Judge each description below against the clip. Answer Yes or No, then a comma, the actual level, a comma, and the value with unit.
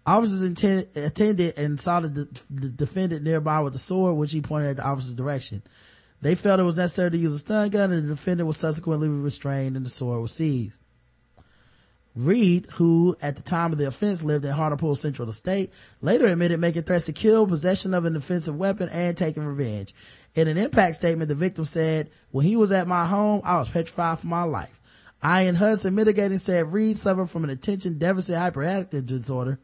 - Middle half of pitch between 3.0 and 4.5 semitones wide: Yes, average, 4.2 semitones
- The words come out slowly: No, average, 200 wpm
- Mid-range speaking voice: Yes, medium, 165 Hz